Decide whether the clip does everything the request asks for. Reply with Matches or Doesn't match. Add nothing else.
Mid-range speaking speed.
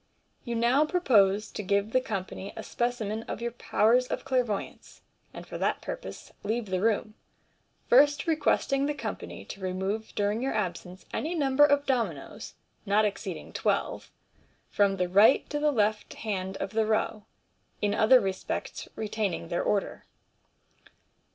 Matches